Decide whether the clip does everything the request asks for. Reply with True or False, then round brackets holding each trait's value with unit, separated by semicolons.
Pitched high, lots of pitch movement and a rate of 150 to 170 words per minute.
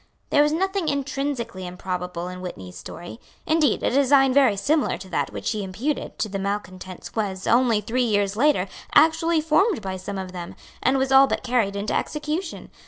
False (235 Hz; 7.4 semitones; 180 wpm)